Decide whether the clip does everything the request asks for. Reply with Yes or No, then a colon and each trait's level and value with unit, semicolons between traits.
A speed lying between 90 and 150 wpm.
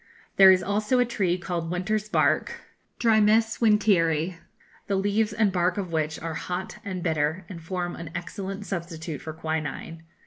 No: average, 160 wpm